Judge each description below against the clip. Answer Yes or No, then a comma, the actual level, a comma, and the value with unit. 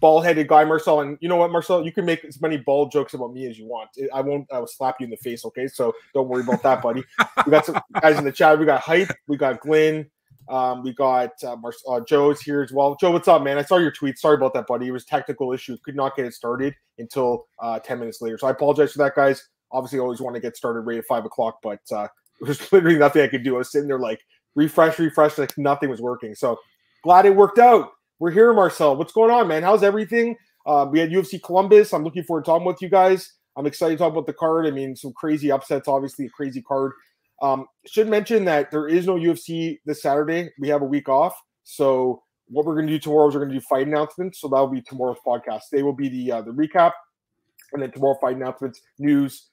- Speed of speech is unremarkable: No, fast, 260 wpm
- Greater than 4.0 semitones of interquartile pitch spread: No, average, 3.6 semitones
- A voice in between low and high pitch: Yes, medium, 145 Hz